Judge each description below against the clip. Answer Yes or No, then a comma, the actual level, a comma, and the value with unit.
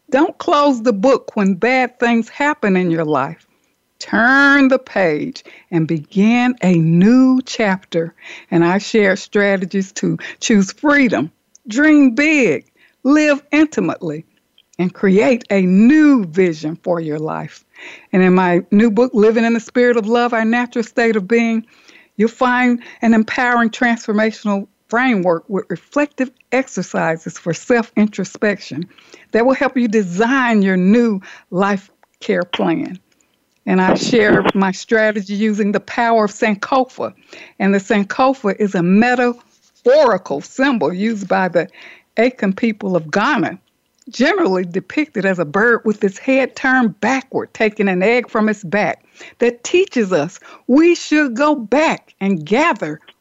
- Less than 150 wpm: Yes, average, 140 wpm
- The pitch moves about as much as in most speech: Yes, average, 4.6 semitones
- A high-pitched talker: Yes, high, 225 Hz